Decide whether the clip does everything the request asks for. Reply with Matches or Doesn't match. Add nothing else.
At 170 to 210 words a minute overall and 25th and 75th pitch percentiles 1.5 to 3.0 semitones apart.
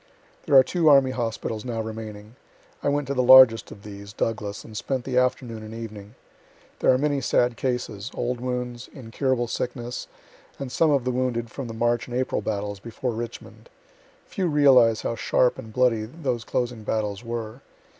Matches